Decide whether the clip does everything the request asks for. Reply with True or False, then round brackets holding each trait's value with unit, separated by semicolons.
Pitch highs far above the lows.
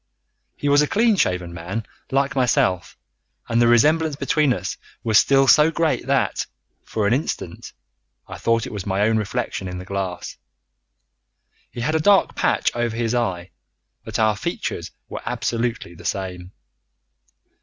True (6.4 semitones)